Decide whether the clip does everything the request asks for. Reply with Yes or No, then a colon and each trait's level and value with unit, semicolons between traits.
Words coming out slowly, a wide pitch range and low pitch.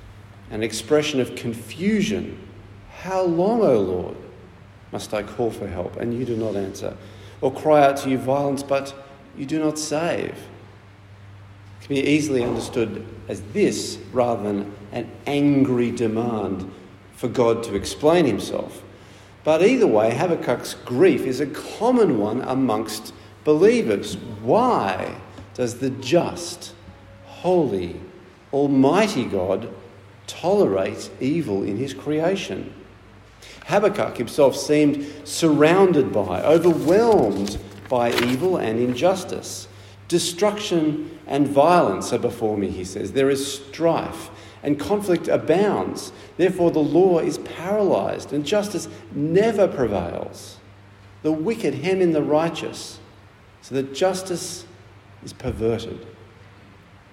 Yes: slow, 120 wpm; wide, 7.0 semitones; low, 120 Hz